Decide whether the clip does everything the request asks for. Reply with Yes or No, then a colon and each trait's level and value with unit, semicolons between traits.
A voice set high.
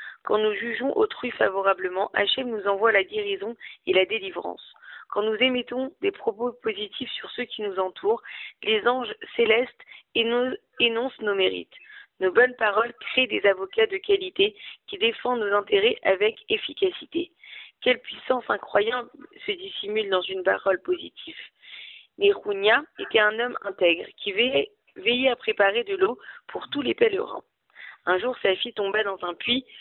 Yes: high, 245 Hz